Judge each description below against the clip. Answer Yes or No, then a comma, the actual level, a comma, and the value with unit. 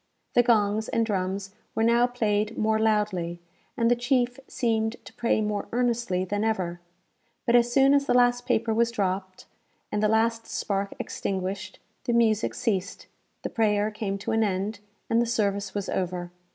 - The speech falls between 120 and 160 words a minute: No, average, 170 wpm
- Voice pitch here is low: No, high, 220 Hz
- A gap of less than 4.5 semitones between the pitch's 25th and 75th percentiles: Yes, average, 2.9 semitones